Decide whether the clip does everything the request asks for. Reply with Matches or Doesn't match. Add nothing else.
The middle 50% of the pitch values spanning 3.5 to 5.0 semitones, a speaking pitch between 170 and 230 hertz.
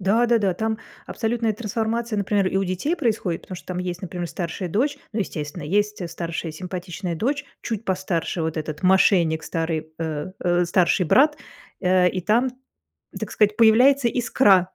Matches